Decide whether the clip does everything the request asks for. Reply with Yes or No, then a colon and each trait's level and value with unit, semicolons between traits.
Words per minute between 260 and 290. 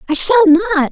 No: average, 200 wpm